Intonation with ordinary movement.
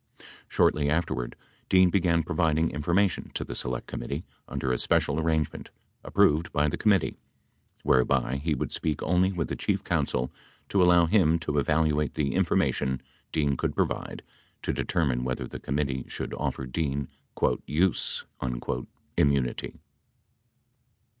Yes: average, 3.5 semitones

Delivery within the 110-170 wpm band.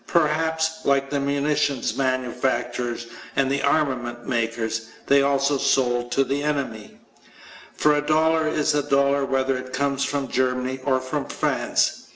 Yes: average, 140 wpm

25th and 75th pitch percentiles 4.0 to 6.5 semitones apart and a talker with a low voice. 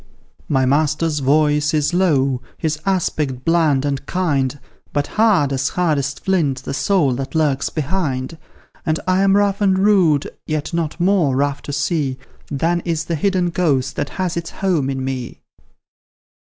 No: average, 4.3 semitones; medium, 155 Hz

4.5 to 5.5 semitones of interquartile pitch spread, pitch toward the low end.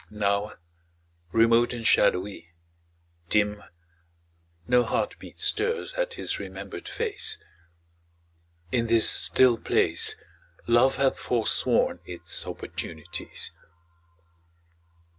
No: average, 3.7 semitones; low, 115 Hz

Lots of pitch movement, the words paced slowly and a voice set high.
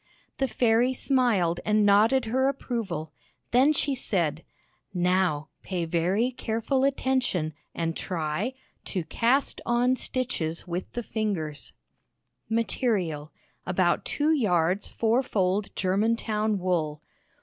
Yes: wide, 6.0 semitones; slow, 110 wpm; high, 210 Hz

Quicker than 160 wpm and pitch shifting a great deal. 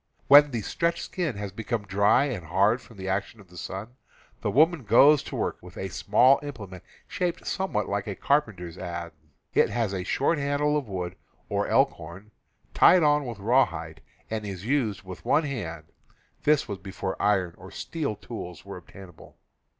Yes: average, 180 wpm; wide, 6.9 semitones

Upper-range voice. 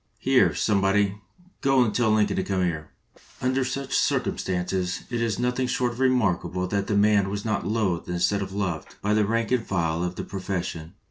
No: low, 100 Hz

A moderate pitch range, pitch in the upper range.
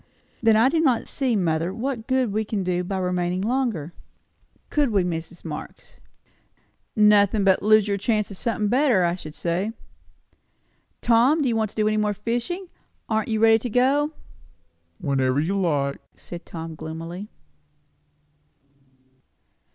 Yes: average, 4.8 semitones; high, 210 Hz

